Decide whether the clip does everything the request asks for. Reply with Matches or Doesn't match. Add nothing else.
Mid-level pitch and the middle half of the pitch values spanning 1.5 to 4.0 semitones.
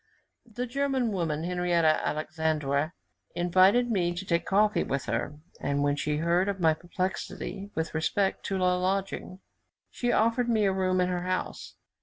Matches